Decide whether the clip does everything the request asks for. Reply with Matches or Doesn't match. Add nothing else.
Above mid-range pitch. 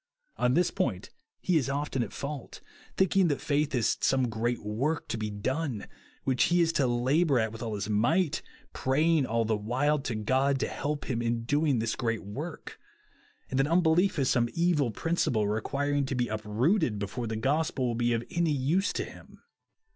Doesn't match